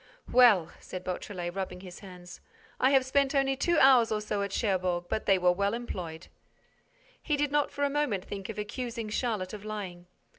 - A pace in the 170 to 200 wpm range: Yes, average, 190 wpm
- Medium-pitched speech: No, high, 210 Hz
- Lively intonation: Yes, wide, 5.9 semitones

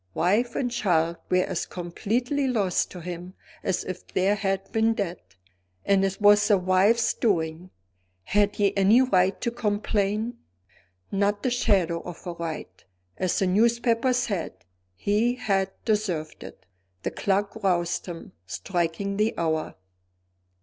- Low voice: No, high, 195 Hz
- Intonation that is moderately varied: Yes, average, 3.7 semitones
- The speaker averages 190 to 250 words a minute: No, average, 140 wpm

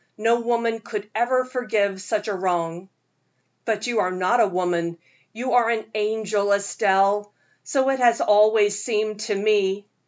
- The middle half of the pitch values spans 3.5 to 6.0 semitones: No, narrow, 2.6 semitones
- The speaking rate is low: No, average, 155 wpm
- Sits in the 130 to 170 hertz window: No, high, 210 Hz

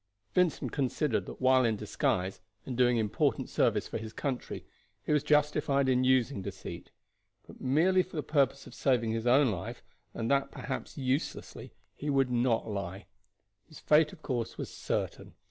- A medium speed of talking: Yes, average, 165 wpm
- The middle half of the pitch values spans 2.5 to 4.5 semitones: Yes, average, 3.9 semitones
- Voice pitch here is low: Yes, low, 130 Hz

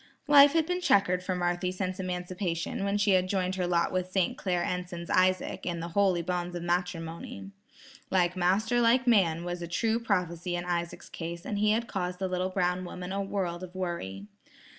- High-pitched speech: No, medium, 180 Hz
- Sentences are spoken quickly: No, average, 185 wpm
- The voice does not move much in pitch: Yes, narrow, 1.9 semitones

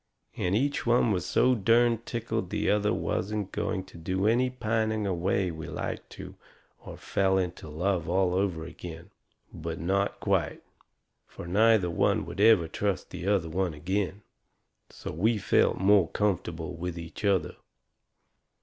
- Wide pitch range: No, average, 3.6 semitones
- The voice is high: No, very low, 95 Hz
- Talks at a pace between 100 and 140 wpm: No, average, 155 wpm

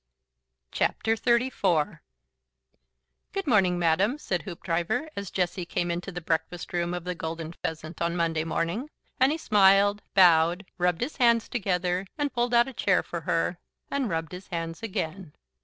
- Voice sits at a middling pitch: Yes, medium, 180 Hz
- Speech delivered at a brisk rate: No, average, 155 wpm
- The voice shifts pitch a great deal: No, average, 4.7 semitones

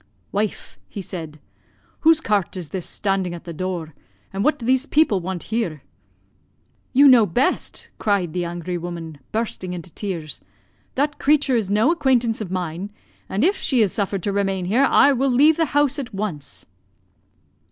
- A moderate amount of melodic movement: No, wide, 6.5 semitones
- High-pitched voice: Yes, high, 200 Hz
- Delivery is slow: No, average, 170 wpm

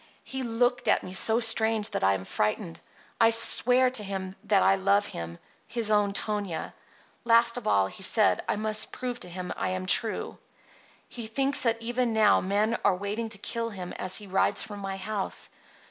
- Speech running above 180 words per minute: Yes, average, 190 wpm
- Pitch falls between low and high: No, high, 210 Hz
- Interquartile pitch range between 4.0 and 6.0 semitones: No, average, 3.2 semitones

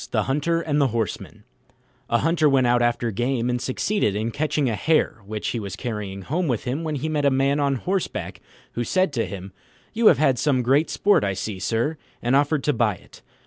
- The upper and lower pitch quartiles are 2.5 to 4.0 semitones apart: No, average, 4.6 semitones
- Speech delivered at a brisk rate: Yes, fast, 215 wpm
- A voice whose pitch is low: Yes, low, 130 Hz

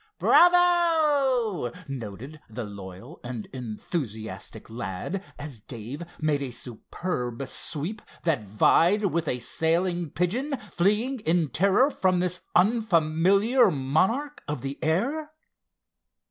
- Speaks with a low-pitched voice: No, medium, 165 Hz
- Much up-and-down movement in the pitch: Yes, wide, 9.0 semitones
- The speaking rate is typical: No, slow, 105 wpm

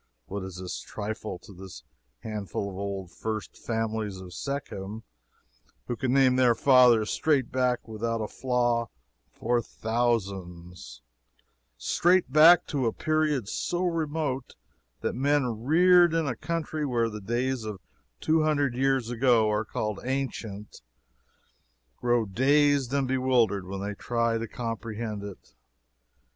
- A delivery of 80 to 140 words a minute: Yes, slow, 135 wpm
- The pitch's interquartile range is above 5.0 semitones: No, average, 4.3 semitones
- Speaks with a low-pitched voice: Yes, low, 120 Hz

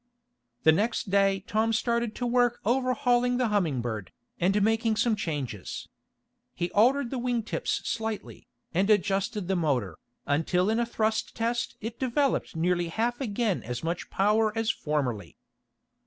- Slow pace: No, average, 150 wpm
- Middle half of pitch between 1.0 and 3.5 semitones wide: No, average, 5.3 semitones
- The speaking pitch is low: No, high, 215 Hz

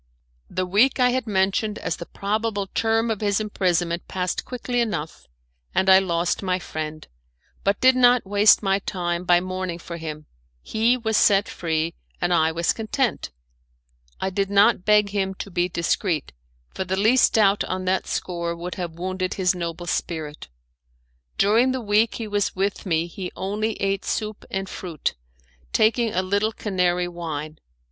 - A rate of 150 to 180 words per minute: Yes, average, 165 wpm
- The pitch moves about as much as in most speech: Yes, average, 3.4 semitones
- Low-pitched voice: No, high, 190 Hz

